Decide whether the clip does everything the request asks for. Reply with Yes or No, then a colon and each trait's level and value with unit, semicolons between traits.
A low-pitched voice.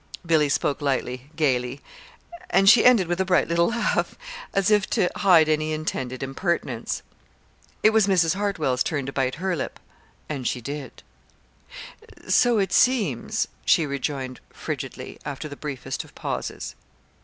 No: medium, 155 Hz